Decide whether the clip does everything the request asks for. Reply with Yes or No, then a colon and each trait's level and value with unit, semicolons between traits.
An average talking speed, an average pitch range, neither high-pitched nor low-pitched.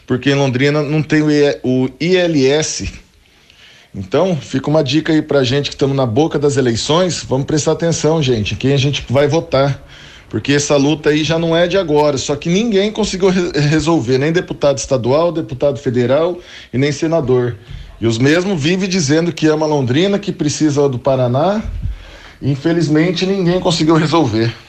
Yes: average, 170 wpm; average, 3.8 semitones; medium, 150 Hz